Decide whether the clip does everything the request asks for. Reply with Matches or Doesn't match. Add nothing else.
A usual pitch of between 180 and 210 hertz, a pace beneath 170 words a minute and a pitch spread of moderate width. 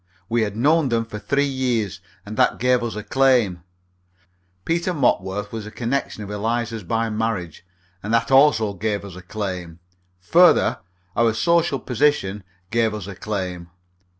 Doesn't match